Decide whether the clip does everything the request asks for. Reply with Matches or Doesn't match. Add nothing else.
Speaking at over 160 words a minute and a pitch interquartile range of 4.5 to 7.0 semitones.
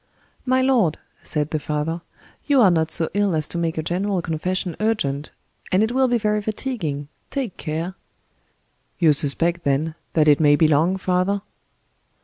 Doesn't match